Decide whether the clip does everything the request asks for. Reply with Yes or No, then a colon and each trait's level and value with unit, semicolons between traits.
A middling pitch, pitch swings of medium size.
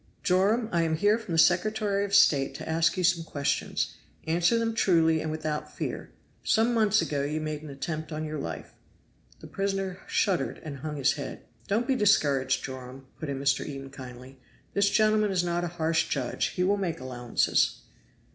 No: medium, 165 Hz; wide, 5.9 semitones